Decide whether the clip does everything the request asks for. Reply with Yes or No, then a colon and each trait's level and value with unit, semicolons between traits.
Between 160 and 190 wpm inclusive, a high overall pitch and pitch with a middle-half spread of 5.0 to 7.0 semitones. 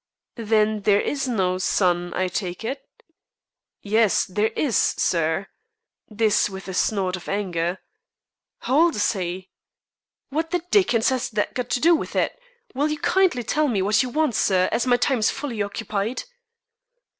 Yes: average, 165 wpm; high, 215 Hz; average, 5.3 semitones